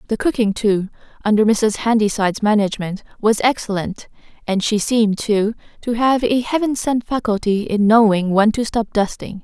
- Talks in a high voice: Yes, high, 215 Hz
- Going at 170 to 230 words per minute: No, average, 160 wpm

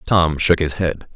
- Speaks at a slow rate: No, fast, 205 wpm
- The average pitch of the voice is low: Yes, very low, 80 Hz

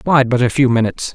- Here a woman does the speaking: No, male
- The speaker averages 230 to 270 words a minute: Yes, fast, 260 wpm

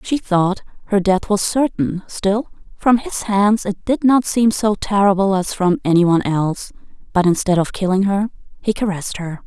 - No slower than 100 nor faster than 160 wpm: No, average, 175 wpm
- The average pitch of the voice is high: Yes, high, 200 Hz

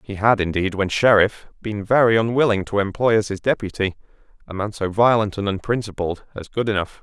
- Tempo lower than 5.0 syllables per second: No, 5.8 syllables/s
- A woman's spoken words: No, male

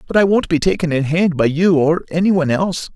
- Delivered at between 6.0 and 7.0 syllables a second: Yes, 6.3 syllables/s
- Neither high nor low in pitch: Yes, medium, 165 Hz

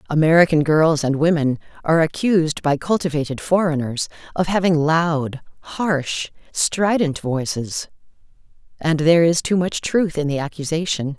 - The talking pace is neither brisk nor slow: No, slow, 130 wpm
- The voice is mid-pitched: Yes, medium, 160 Hz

